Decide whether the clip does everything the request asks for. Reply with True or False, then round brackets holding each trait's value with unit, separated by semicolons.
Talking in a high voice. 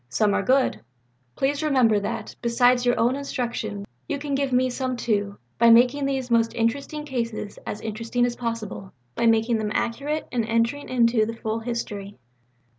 True (235 Hz)